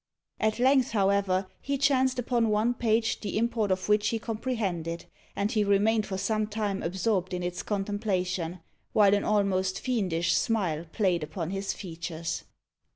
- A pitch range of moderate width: Yes, average, 3.3 semitones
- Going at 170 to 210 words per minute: No, average, 155 wpm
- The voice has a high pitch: Yes, high, 205 Hz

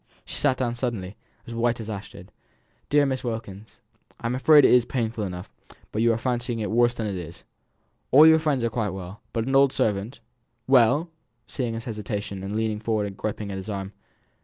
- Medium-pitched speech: No, low, 115 Hz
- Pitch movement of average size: Yes, average, 3.3 semitones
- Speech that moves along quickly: Yes, fast, 210 wpm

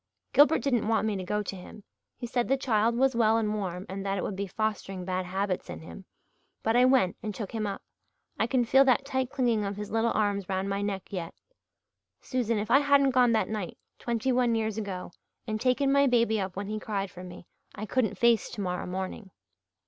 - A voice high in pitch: Yes, high, 215 Hz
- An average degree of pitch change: Yes, average, 3.7 semitones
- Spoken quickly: Yes, fast, 220 wpm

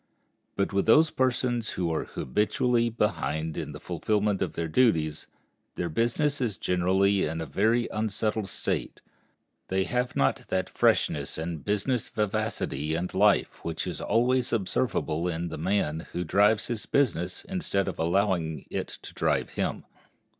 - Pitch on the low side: Yes, low, 100 Hz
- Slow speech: No, average, 150 wpm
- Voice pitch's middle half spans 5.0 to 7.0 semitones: Yes, wide, 5.6 semitones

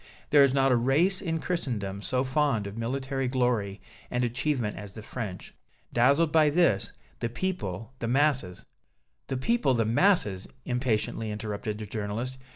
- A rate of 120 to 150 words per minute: No, average, 160 wpm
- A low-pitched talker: Yes, low, 125 Hz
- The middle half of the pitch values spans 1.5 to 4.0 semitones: No, average, 4.7 semitones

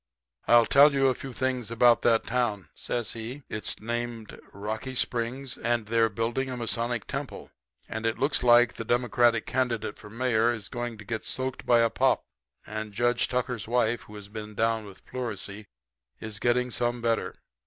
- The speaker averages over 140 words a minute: Yes, average, 175 wpm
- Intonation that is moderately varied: No, narrow, 1.9 semitones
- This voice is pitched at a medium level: No, low, 115 Hz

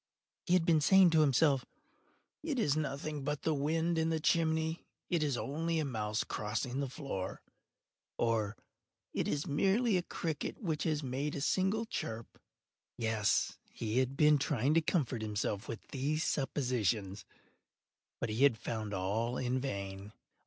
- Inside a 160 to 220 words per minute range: No, average, 150 wpm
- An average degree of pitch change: No, wide, 5.8 semitones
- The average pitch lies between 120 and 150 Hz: Yes, medium, 140 Hz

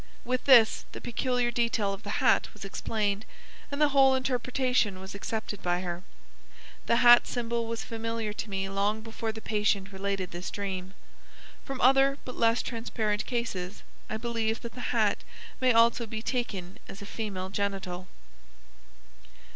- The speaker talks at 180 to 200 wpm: No, average, 155 wpm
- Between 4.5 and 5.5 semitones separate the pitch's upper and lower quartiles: No, average, 3.3 semitones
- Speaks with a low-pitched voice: No, high, 220 Hz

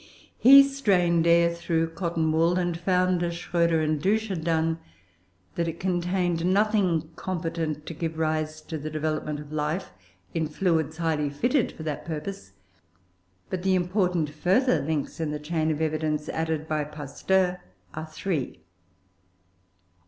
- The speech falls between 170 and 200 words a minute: No, average, 145 wpm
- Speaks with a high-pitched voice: No, medium, 165 Hz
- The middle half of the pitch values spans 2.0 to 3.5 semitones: Yes, narrow, 2.5 semitones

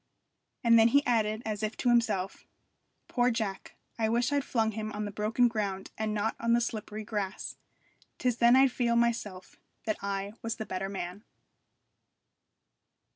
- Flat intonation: Yes, narrow, 2.3 semitones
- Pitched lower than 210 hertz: No, high, 220 Hz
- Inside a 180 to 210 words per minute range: No, average, 165 wpm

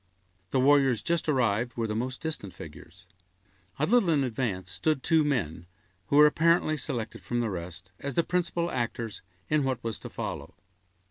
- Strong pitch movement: Yes, wide, 5.9 semitones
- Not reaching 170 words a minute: No, average, 175 wpm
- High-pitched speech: No, low, 130 Hz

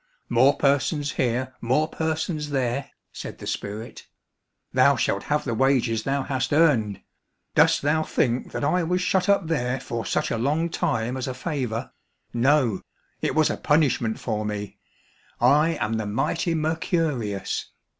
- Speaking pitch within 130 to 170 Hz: Yes, low, 135 Hz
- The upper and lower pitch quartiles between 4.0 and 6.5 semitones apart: Yes, average, 5.0 semitones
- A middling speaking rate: Yes, average, 155 wpm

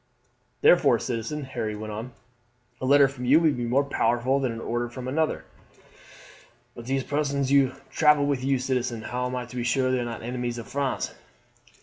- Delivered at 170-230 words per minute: Yes, average, 195 wpm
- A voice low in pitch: Yes, low, 130 Hz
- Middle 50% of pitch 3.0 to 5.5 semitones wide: No, narrow, 2.5 semitones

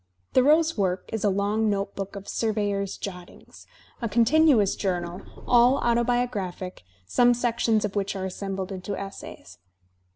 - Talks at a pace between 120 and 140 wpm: Yes, slow, 135 wpm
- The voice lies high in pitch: Yes, high, 205 Hz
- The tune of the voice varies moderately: Yes, average, 3.6 semitones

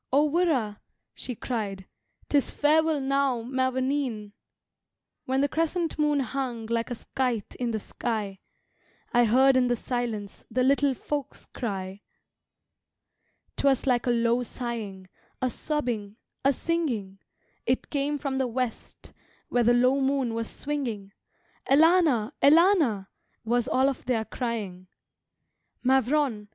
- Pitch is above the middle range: Yes, very high, 250 Hz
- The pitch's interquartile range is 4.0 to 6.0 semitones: No, average, 3.6 semitones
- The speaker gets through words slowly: Yes, slow, 125 wpm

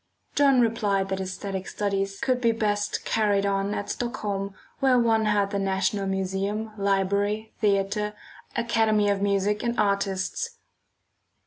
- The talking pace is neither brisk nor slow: No, slow, 130 wpm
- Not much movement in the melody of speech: Yes, narrow, 2.1 semitones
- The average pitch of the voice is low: No, high, 205 Hz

